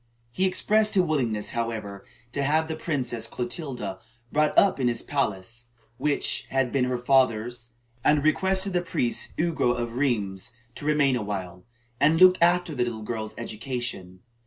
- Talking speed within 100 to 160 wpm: Yes, average, 150 wpm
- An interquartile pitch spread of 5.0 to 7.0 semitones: Yes, average, 5.3 semitones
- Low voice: Yes, low, 125 Hz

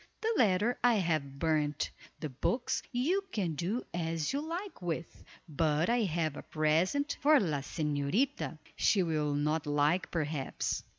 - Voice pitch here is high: No, medium, 165 Hz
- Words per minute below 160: Yes, average, 145 wpm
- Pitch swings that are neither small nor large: No, wide, 7.5 semitones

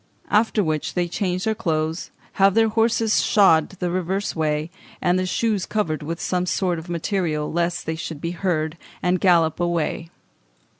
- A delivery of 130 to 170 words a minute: Yes, average, 160 wpm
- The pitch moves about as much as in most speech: Yes, average, 3.2 semitones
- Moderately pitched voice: Yes, medium, 175 Hz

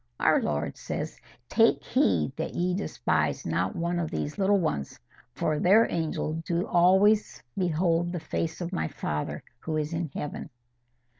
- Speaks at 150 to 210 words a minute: Yes, average, 155 wpm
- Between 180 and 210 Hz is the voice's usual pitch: No, medium, 165 Hz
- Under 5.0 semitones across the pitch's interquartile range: Yes, average, 3.3 semitones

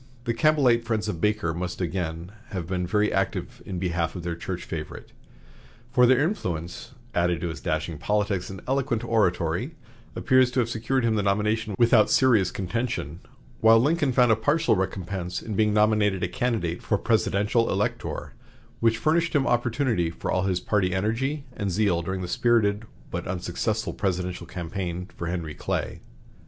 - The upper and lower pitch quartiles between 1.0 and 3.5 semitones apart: No, average, 4.7 semitones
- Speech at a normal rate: Yes, average, 165 wpm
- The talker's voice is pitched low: Yes, low, 105 Hz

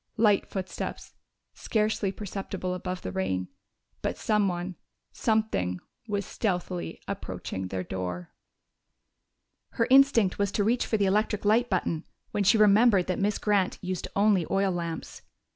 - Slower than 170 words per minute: Yes, slow, 135 wpm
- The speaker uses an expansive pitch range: No, average, 3.3 semitones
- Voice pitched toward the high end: Yes, high, 195 Hz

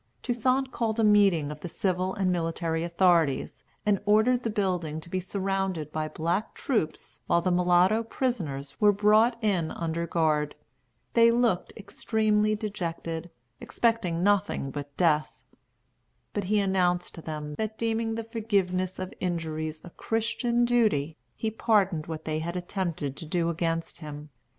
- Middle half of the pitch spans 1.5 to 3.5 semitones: No, average, 4.7 semitones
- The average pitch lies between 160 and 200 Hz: Yes, medium, 185 Hz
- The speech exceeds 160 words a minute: No, average, 150 wpm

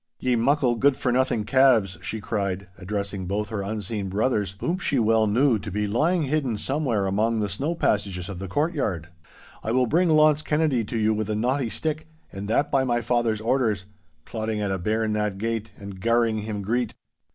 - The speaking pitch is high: No, low, 110 Hz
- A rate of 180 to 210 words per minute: Yes, average, 190 wpm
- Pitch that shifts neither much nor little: Yes, average, 4.2 semitones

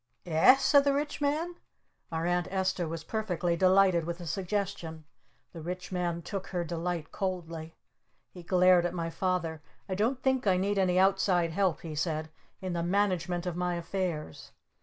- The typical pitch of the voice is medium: Yes, medium, 180 Hz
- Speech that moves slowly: No, average, 170 wpm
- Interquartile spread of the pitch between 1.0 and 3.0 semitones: Yes, narrow, 2.5 semitones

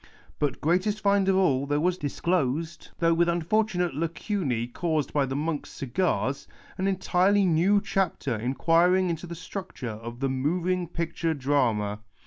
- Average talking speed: Yes, average, 160 wpm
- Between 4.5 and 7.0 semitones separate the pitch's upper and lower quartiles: Yes, average, 4.9 semitones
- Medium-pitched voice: Yes, medium, 165 Hz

